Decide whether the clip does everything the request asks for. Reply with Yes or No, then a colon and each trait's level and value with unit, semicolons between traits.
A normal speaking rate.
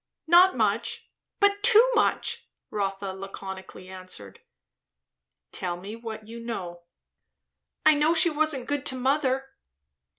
No: slow, 120 wpm